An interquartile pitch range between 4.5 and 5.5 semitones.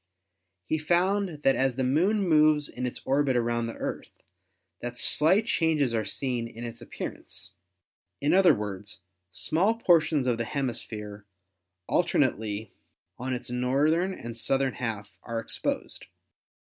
Yes: average, 5.1 semitones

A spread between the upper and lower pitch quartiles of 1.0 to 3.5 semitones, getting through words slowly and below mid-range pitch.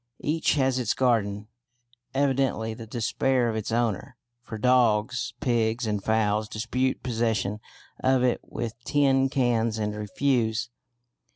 Yes: average, 2.8 semitones; slow, 125 wpm; low, 120 Hz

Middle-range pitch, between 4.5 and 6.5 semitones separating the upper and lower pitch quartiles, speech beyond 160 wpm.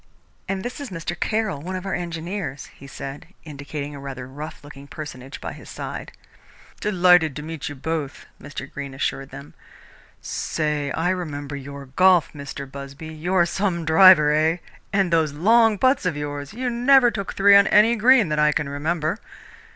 Yes: medium, 160 Hz; average, 4.9 semitones; average, 175 wpm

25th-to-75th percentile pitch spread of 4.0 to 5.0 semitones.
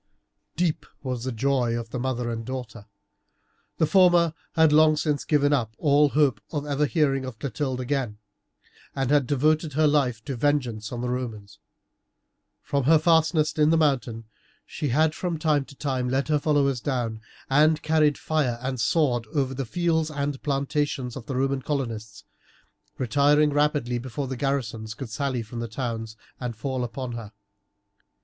No: average, 3.6 semitones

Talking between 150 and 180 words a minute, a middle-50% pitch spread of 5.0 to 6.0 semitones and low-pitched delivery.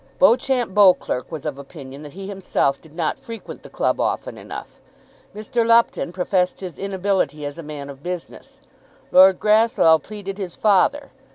No: average, 160 wpm; average, 5.3 semitones; medium, 185 Hz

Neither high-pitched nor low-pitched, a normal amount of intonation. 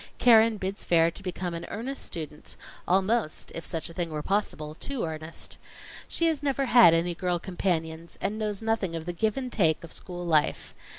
Yes: medium, 180 Hz; average, 4.9 semitones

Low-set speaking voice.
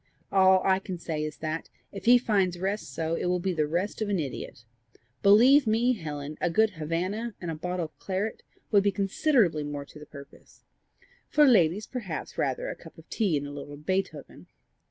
No: medium, 185 Hz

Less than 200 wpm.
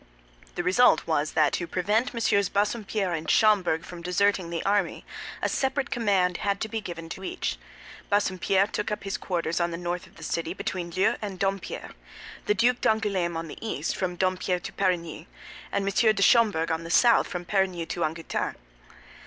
Yes: average, 185 wpm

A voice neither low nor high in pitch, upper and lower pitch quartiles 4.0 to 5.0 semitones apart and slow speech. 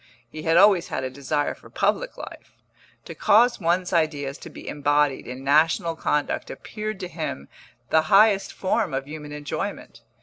No: medium, 155 Hz; average, 4.4 semitones; average, 165 wpm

